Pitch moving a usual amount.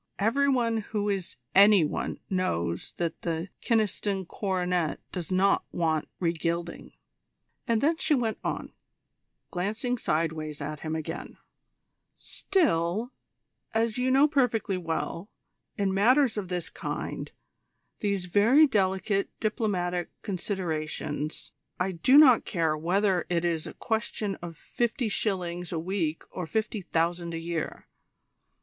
Yes: average, 4.7 semitones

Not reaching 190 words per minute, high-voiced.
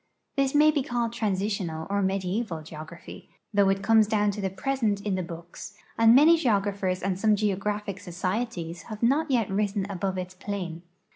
Yes: average, 170 wpm; high, 200 Hz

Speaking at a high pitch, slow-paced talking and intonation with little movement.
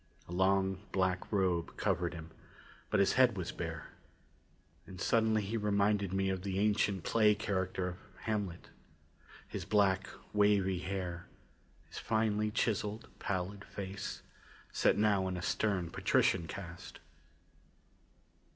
No: very low, 95 Hz; slow, 125 wpm; narrow, 2.3 semitones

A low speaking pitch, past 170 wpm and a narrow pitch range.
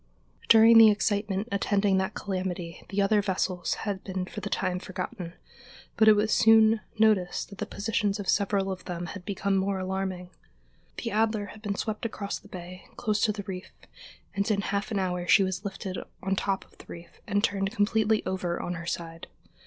No: high, 195 Hz; average, 195 wpm; narrow, 2.2 semitones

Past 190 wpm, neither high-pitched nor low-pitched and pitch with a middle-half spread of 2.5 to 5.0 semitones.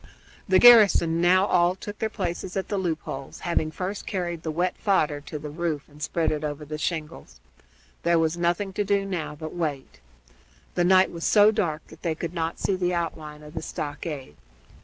Yes: average, 200 wpm; medium, 170 Hz; average, 3.4 semitones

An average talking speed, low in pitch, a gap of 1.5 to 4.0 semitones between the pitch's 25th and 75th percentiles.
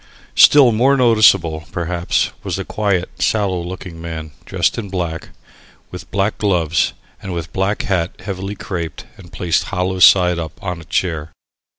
Yes: average, 160 wpm; very low, 90 Hz; average, 2.9 semitones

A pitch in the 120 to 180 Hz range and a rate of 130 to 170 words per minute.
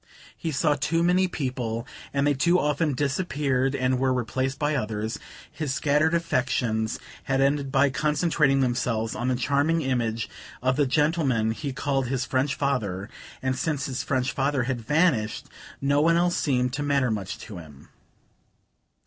Yes: low, 135 Hz; average, 160 wpm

